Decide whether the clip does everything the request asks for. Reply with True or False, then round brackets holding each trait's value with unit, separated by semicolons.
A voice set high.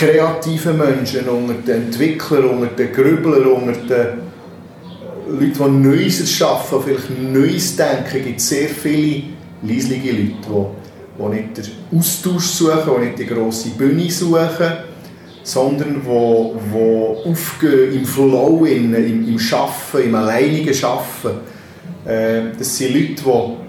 False (135 Hz)